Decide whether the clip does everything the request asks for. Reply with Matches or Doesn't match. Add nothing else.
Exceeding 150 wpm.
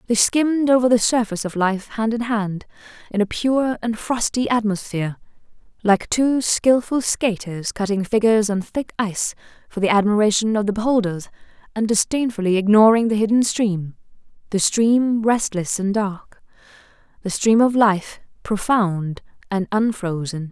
Doesn't match